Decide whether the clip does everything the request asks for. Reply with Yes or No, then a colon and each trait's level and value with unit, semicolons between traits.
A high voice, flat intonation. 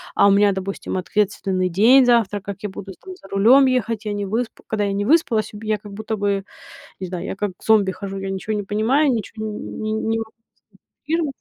Yes: high, 210 Hz; narrow, 2.2 semitones